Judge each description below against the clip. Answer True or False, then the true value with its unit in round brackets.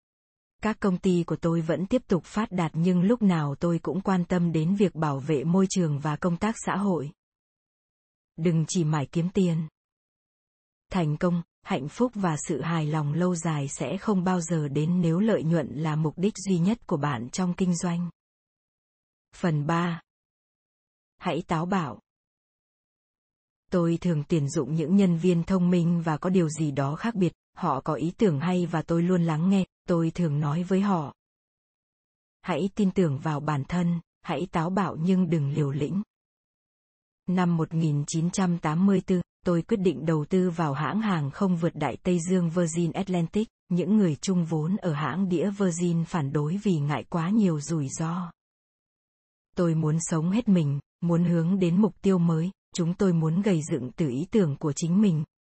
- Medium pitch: True (175 Hz)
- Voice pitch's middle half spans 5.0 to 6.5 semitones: False (2.8 semitones)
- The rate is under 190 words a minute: True (180 wpm)